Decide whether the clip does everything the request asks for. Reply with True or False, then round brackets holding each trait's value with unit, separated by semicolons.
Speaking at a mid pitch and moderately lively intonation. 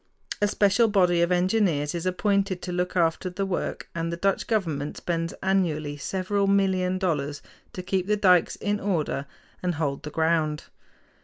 True (180 Hz; 3.0 semitones)